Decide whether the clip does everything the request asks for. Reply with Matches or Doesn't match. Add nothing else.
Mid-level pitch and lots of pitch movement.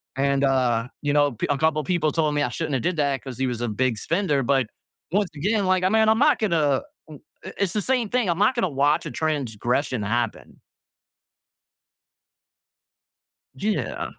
Matches